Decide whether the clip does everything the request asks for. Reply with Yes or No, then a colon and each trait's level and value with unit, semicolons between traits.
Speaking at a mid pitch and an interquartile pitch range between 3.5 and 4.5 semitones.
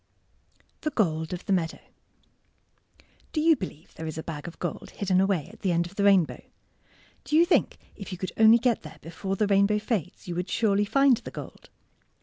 No: high, 195 Hz; average, 4.1 semitones